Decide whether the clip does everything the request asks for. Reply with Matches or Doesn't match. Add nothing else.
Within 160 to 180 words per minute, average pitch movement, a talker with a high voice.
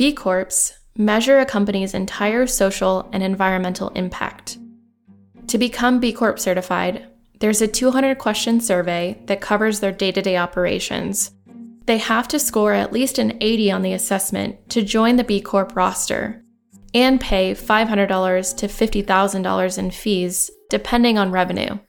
Doesn't match